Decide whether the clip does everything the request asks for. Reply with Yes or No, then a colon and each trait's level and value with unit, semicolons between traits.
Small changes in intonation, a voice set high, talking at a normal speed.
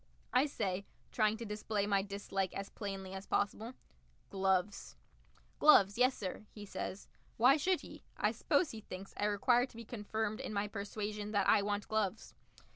Yes: narrow, 1.9 semitones; high, 205 Hz; average, 165 wpm